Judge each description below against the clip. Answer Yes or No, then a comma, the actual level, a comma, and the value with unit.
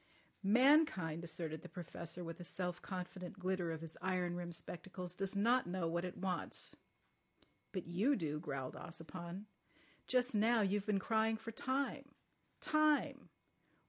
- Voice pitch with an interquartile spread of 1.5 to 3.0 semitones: No, average, 4.1 semitones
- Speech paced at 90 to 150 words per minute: Yes, average, 140 wpm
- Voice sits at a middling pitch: Yes, medium, 180 Hz